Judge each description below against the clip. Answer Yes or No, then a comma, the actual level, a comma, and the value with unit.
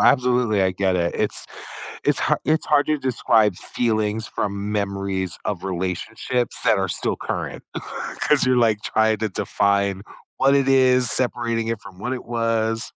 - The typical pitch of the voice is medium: No, low, 110 Hz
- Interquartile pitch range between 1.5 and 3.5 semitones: No, average, 3.9 semitones